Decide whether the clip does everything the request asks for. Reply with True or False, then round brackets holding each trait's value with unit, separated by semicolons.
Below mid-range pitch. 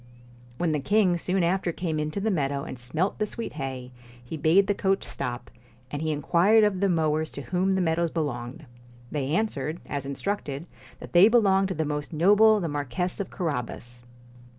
False (165 Hz)